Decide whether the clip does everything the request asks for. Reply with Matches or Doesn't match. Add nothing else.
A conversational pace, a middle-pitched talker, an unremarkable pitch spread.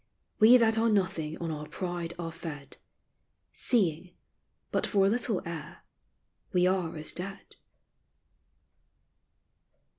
Doesn't match